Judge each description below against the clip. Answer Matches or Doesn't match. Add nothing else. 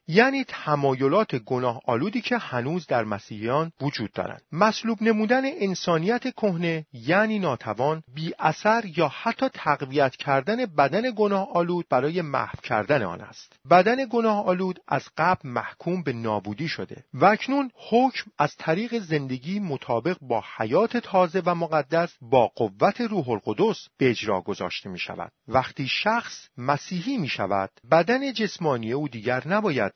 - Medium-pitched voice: Matches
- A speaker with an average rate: Matches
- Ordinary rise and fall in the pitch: Doesn't match